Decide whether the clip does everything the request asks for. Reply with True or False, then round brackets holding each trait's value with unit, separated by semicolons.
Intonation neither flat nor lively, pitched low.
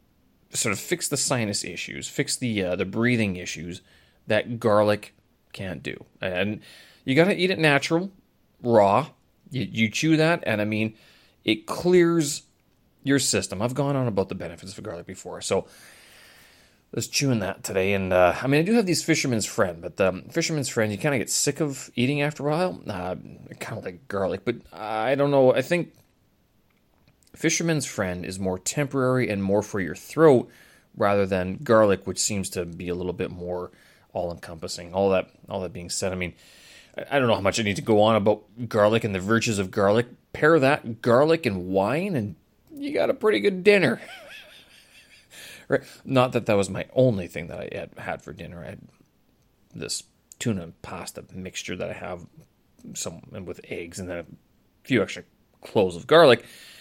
False (6.8 semitones; 110 Hz)